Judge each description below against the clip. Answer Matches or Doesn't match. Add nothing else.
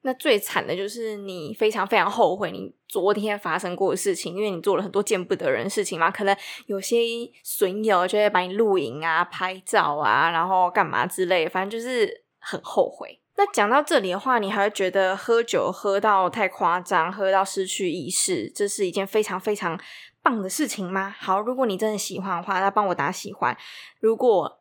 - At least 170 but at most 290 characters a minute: Doesn't match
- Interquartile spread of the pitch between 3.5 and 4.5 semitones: Matches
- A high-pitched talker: Matches